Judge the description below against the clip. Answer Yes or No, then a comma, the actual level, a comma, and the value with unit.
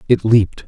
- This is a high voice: No, low, 110 Hz